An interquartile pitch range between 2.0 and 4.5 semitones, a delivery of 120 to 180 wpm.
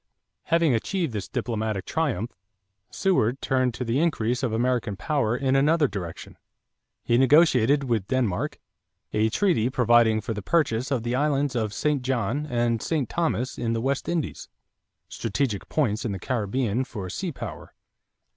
Yes: average, 4.1 semitones; average, 155 wpm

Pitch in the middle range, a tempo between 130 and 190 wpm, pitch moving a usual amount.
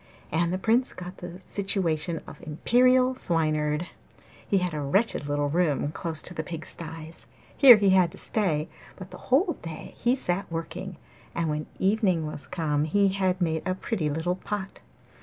Yes: medium, 175 Hz; average, 170 wpm; average, 3.8 semitones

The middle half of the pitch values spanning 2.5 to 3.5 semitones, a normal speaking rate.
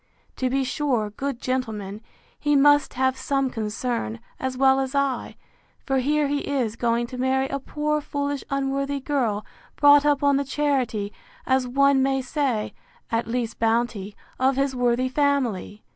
Yes: average, 2.8 semitones; average, 160 wpm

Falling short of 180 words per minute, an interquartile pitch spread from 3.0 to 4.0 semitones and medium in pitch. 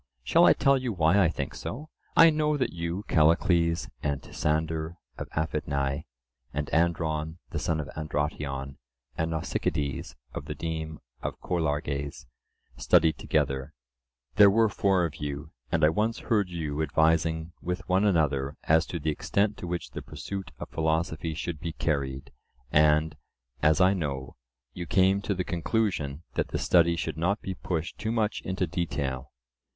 No: average, 160 wpm; average, 3.4 semitones; very low, 80 Hz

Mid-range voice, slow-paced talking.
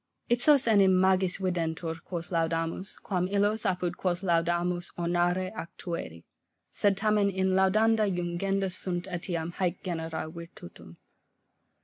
Yes: medium, 180 Hz; slow, 120 wpm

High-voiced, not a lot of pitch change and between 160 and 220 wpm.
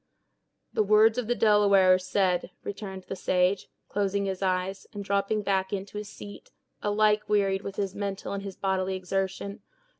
Yes: high, 195 Hz; narrow, 1.3 semitones; average, 170 wpm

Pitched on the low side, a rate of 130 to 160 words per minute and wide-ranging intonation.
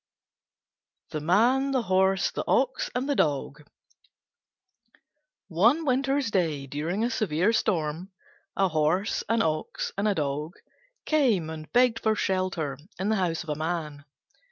No: medium, 185 Hz; average, 140 wpm; wide, 6.6 semitones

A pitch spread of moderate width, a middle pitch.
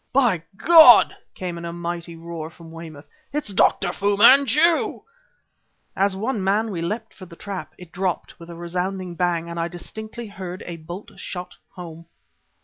Yes: average, 3.5 semitones; medium, 180 Hz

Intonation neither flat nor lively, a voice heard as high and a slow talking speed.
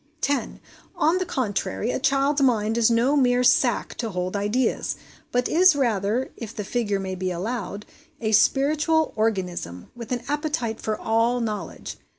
No: average, 4.6 semitones; high, 235 Hz; average, 160 wpm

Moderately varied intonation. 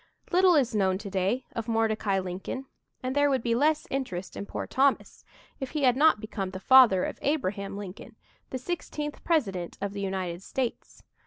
No: wide, 5.9 semitones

